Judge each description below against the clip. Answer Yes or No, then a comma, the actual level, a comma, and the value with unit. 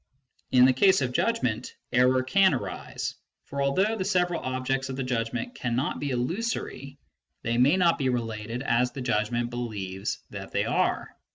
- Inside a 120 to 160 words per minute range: No, average, 170 wpm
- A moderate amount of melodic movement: Yes, average, 3.3 semitones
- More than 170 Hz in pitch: No, low, 130 Hz